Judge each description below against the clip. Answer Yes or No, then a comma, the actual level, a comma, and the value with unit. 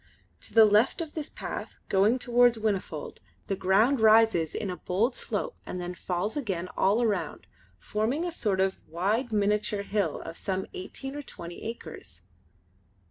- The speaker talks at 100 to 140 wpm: No, average, 160 wpm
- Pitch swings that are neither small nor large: Yes, average, 4.3 semitones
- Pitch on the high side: Yes, high, 210 Hz